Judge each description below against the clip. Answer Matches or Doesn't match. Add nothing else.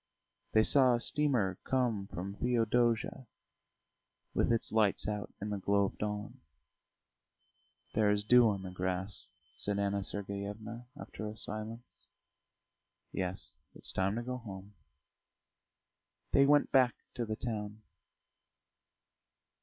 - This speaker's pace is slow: Matches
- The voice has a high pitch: Doesn't match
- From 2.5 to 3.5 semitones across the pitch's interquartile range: Matches